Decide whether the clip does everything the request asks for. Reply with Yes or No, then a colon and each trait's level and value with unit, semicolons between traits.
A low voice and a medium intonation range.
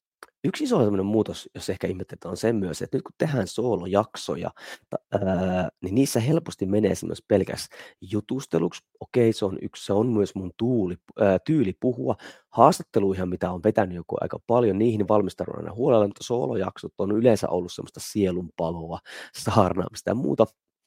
Yes: low, 100 Hz; average, 3.3 semitones